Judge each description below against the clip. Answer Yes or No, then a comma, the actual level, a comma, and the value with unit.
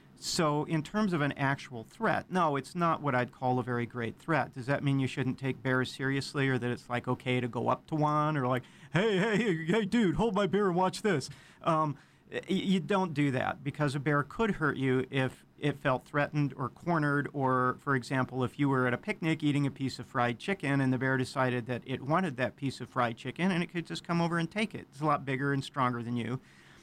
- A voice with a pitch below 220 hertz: Yes, medium, 140 Hz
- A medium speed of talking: No, fast, 240 wpm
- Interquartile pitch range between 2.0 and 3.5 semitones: No, average, 4.2 semitones